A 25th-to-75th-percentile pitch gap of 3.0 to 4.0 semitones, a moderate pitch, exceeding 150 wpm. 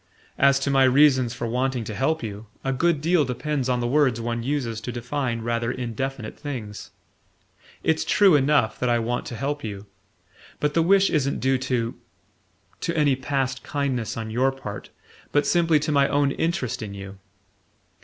No: average, 3.7 semitones; low, 130 Hz; average, 175 wpm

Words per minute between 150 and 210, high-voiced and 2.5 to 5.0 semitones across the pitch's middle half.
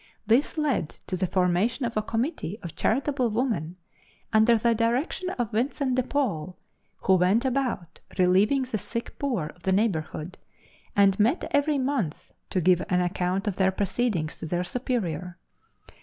No: average, 155 wpm; high, 215 Hz; wide, 5.6 semitones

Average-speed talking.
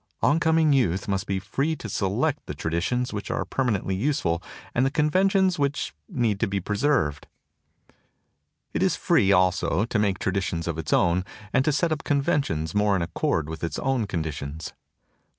Yes: average, 170 wpm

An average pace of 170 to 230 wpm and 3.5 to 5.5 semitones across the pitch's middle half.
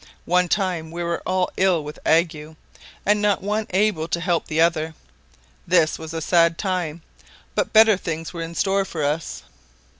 No: average, 175 wpm; average, 2.7 semitones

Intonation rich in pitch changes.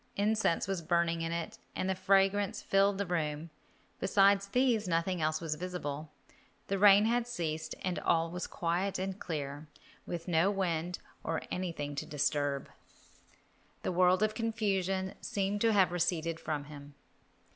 No: average, 3.4 semitones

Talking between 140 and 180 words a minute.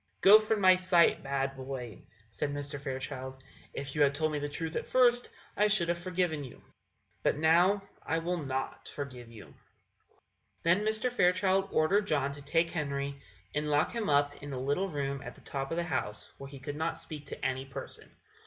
No: average, 190 wpm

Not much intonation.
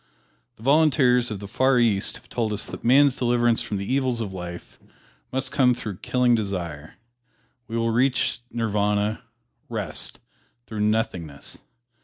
No: average, 3.5 semitones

